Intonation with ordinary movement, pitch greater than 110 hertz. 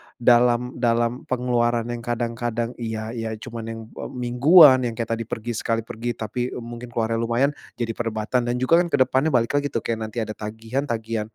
No: narrow, 1.5 semitones; low, 120 Hz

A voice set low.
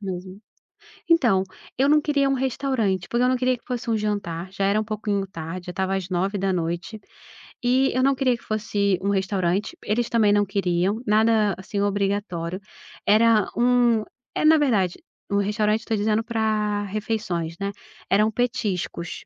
No: high, 210 Hz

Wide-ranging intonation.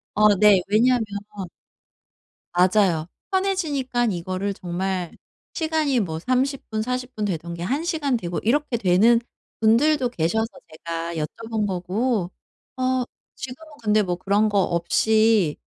Yes: wide, 5.9 semitones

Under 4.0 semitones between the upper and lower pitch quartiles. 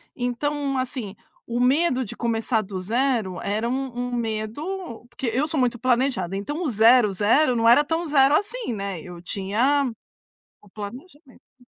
No: average, 4.3 semitones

